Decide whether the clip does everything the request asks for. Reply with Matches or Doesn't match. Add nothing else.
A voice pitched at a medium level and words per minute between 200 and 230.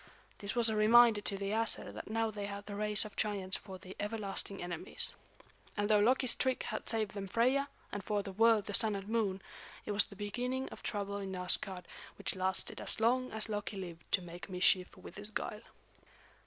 Doesn't match